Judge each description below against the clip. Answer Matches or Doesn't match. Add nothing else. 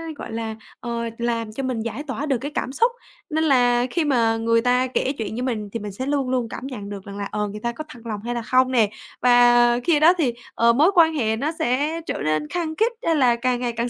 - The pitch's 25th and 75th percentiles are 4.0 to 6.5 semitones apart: Doesn't match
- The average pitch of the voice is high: Matches